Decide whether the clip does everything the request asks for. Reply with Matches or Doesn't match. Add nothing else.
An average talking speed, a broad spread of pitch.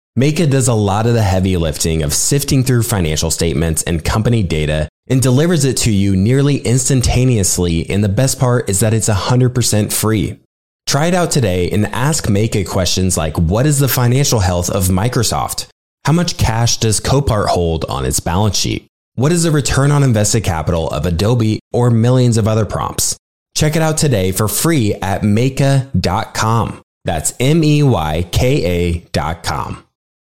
Matches